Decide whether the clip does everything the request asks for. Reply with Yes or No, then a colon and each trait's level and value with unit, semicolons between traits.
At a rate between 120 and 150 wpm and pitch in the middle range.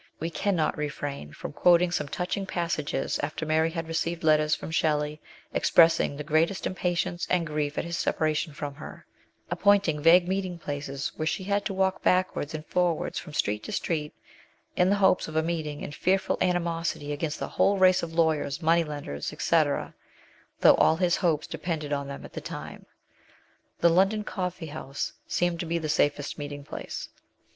No: average, 175 wpm; medium, 165 Hz